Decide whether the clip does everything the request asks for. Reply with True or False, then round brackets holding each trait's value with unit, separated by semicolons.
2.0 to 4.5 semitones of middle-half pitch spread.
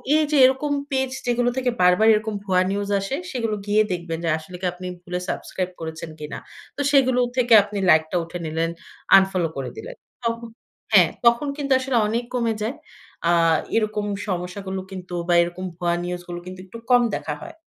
False (5.5 semitones)